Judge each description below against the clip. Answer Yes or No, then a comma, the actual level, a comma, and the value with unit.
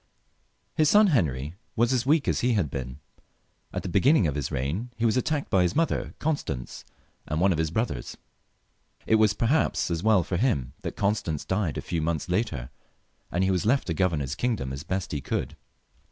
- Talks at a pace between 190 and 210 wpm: Yes, average, 200 wpm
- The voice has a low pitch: Yes, very low, 95 Hz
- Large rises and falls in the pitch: Yes, wide, 7.6 semitones